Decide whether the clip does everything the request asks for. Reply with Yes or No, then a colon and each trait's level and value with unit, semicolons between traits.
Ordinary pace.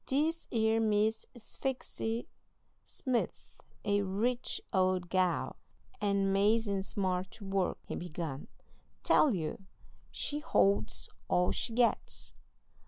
No: slow, 105 wpm